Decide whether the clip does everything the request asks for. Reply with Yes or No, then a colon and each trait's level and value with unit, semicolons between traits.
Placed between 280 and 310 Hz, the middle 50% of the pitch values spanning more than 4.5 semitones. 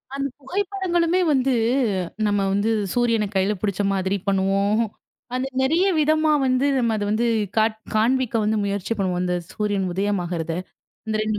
No: high, 215 Hz; average, 4.9 semitones